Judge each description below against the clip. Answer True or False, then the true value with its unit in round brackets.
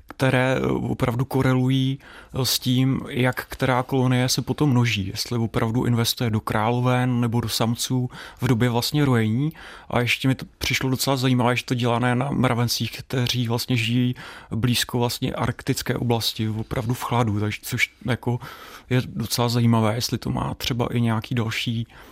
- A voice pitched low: True (125 Hz)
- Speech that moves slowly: False (155 wpm)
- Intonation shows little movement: True (1.7 semitones)